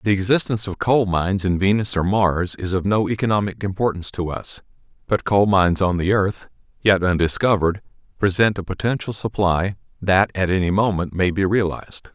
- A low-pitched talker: Yes, low, 100 Hz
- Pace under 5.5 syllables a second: No, 5.6 syllables/s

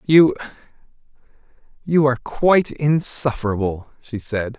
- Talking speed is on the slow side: Yes, slow, 90 wpm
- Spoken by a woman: No, male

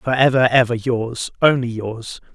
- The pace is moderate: Yes, average, 155 wpm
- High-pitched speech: No, low, 120 Hz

